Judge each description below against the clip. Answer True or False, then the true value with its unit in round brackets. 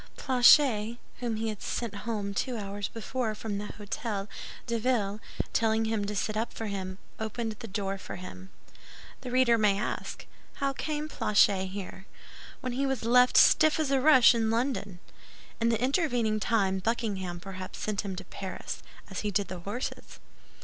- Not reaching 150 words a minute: False (175 wpm)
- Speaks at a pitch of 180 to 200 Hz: False (220 Hz)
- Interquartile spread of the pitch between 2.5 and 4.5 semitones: True (3.4 semitones)